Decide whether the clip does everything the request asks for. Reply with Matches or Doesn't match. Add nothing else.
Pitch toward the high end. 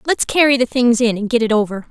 Matches